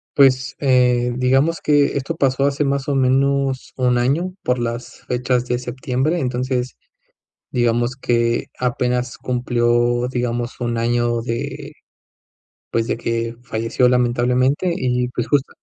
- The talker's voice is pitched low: Yes, low, 125 Hz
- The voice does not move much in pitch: Yes, narrow, 1.9 semitones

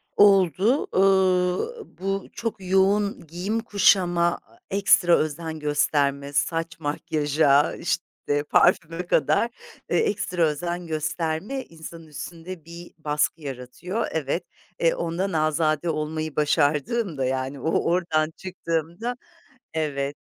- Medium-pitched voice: Yes, medium, 165 Hz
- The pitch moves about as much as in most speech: Yes, average, 3.6 semitones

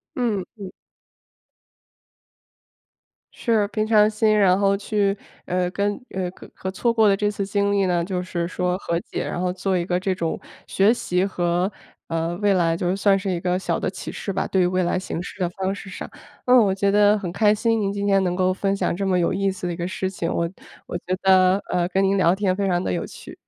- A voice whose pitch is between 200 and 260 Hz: No, high, 190 Hz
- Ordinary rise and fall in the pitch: No, narrow, 2.0 semitones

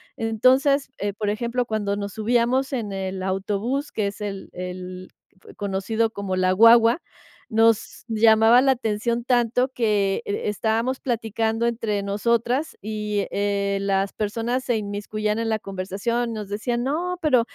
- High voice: Yes, high, 220 Hz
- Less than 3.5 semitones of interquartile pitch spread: Yes, average, 2.8 semitones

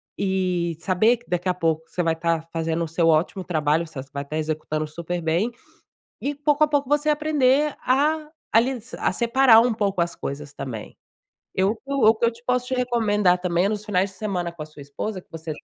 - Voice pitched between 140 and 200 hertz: Yes, medium, 185 Hz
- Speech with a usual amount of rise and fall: No, wide, 6.8 semitones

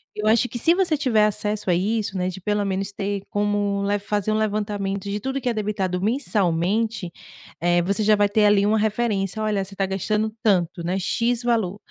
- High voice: Yes, high, 205 Hz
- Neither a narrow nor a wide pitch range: No, narrow, 1.9 semitones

